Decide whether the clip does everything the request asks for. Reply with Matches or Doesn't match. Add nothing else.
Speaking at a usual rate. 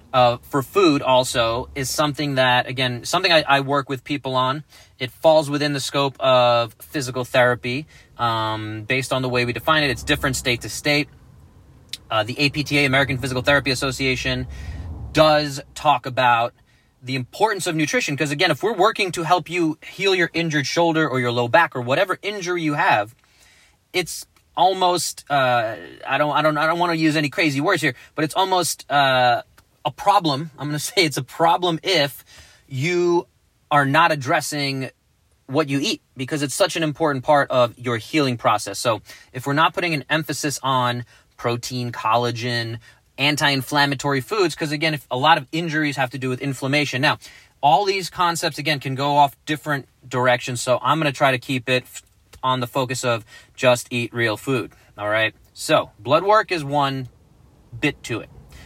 Matches